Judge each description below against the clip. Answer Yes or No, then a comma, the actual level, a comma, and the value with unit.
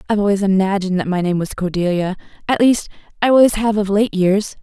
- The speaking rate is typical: Yes, average, 195 wpm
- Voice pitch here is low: No, high, 200 Hz